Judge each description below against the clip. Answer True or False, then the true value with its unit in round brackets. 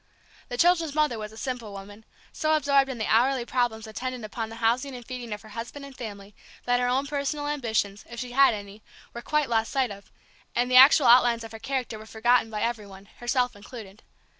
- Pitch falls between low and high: False (240 Hz)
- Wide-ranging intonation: False (3.2 semitones)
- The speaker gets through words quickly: True (215 wpm)